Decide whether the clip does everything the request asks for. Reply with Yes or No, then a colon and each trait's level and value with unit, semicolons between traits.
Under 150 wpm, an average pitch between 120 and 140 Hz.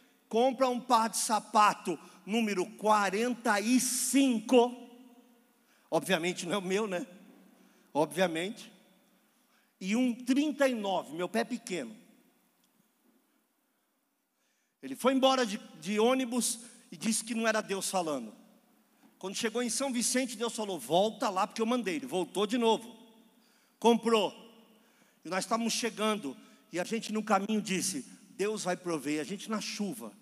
No: average, 135 wpm; high, 230 Hz